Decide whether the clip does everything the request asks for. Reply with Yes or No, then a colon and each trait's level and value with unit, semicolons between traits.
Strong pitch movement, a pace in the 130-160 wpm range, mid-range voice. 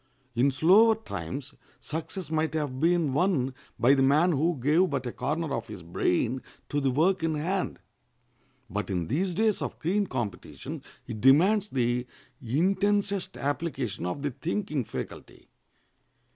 Yes: wide, 5.8 semitones; average, 145 wpm; medium, 150 Hz